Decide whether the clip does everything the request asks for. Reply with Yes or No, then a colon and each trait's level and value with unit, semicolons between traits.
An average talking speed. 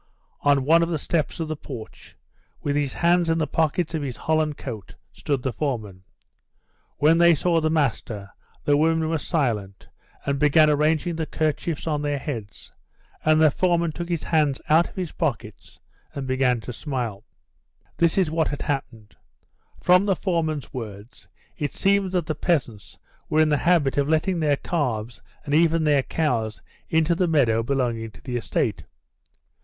Yes: average, 170 wpm